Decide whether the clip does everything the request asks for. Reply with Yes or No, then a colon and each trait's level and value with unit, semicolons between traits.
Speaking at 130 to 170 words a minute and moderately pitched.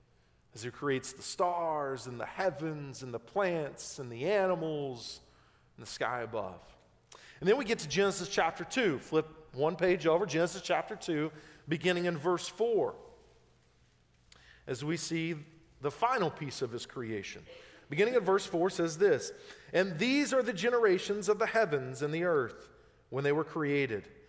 Yes: average, 165 wpm; medium, 165 Hz